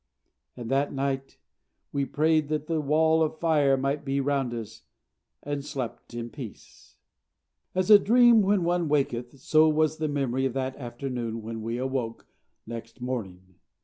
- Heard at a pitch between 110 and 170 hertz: Yes, low, 135 Hz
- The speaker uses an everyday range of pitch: Yes, average, 4.3 semitones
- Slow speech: No, average, 155 wpm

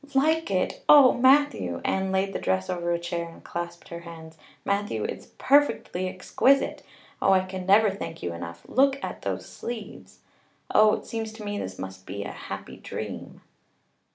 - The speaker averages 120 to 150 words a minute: No, average, 175 wpm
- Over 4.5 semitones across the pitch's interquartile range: Yes, average, 5.0 semitones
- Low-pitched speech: No, high, 190 Hz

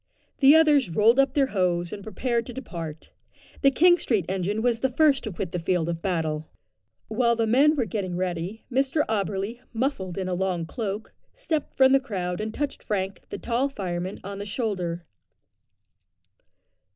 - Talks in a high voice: Yes, high, 210 Hz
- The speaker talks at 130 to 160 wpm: No, average, 175 wpm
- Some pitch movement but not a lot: No, wide, 6.4 semitones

